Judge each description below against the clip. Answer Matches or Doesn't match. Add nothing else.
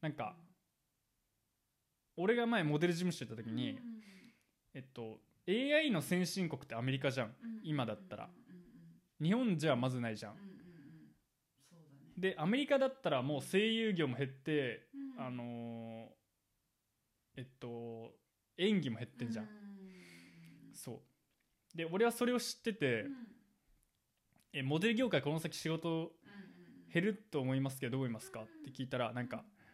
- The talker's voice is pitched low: Doesn't match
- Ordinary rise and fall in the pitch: Doesn't match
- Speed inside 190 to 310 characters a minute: Matches